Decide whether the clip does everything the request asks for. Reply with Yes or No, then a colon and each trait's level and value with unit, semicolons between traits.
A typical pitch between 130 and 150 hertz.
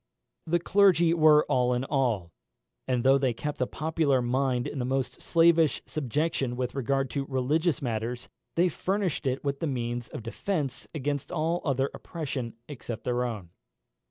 Yes: low, 135 Hz